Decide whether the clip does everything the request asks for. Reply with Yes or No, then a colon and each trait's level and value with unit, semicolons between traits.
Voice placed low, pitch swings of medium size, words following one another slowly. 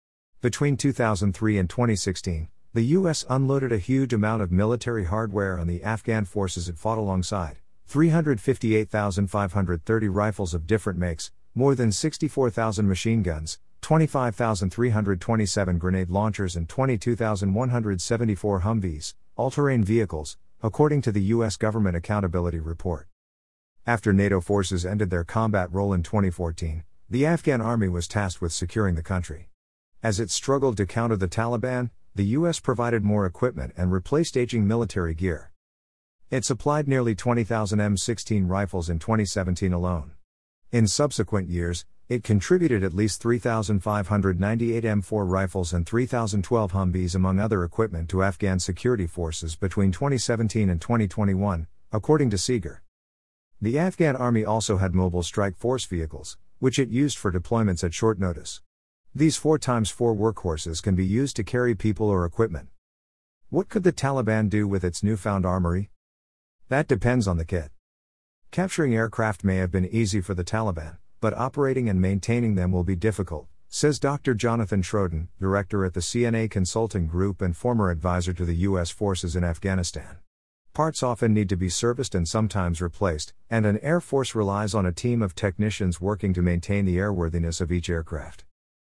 No: low, 100 Hz; average, 4.5 semitones; average, 150 wpm